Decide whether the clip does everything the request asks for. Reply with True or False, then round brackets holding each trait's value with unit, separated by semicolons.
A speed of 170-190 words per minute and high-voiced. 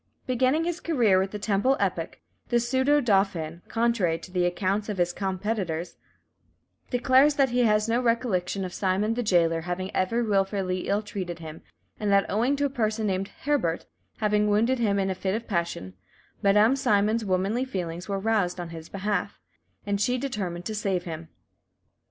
True (175 wpm; 205 Hz)